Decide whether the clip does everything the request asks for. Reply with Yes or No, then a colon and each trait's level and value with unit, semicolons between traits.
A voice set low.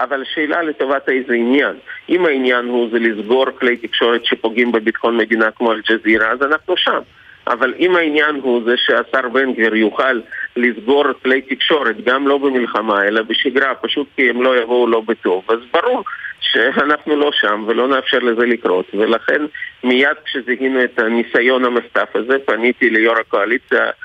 Yes: low, 125 Hz